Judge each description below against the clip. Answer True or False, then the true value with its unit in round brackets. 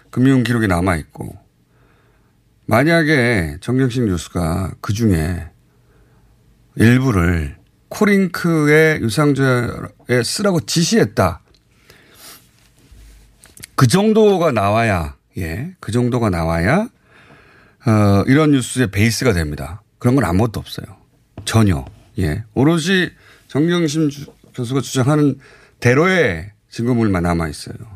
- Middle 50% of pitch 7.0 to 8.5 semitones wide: True (7.4 semitones)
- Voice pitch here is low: True (120 Hz)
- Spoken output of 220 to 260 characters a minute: True (225 characters per minute)